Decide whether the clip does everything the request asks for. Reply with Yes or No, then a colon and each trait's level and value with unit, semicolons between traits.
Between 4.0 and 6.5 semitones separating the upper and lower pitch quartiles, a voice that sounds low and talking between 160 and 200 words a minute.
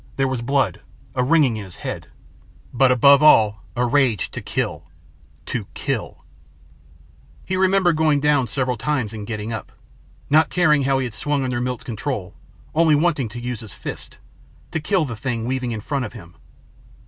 Yes: average, 4.3 semitones; low, 130 Hz; average, 175 wpm